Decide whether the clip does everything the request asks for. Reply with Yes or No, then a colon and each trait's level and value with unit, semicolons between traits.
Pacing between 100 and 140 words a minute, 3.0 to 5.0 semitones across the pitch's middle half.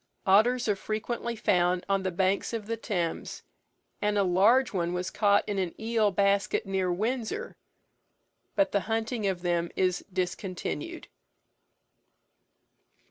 Yes: slow, 135 wpm; average, 3.5 semitones